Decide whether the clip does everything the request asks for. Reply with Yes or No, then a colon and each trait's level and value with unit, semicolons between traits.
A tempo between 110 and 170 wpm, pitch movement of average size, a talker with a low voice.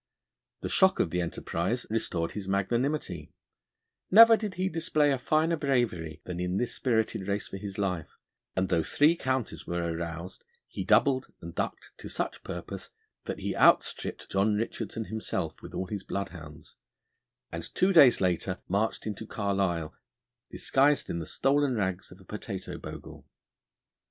No: average, 155 wpm; wide, 6.9 semitones; low, 100 Hz